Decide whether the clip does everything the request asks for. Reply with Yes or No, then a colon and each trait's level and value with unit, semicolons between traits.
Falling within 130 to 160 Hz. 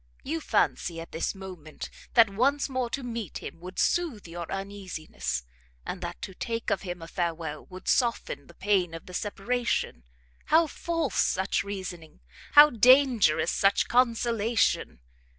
No: high, 195 Hz